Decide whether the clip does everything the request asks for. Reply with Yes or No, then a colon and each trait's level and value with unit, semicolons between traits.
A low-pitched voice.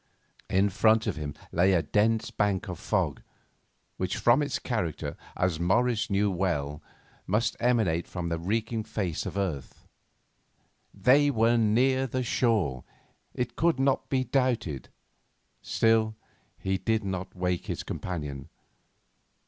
Yes: low, 105 Hz